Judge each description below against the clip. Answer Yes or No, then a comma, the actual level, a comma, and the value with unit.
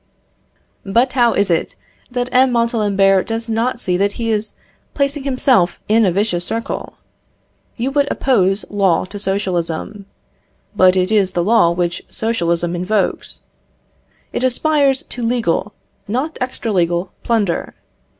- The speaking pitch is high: Yes, high, 210 Hz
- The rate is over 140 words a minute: No, slow, 135 wpm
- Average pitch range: Yes, average, 4.7 semitones